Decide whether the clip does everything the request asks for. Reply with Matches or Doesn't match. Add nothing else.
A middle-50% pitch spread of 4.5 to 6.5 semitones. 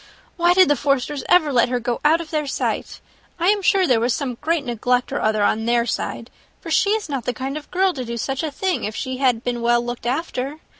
Matches